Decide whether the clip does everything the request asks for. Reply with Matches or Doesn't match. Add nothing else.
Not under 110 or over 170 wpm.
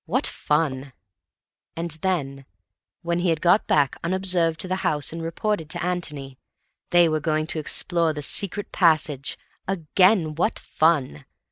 Matches